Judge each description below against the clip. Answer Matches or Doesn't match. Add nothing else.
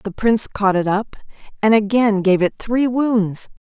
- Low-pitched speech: Doesn't match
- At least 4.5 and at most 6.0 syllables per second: Doesn't match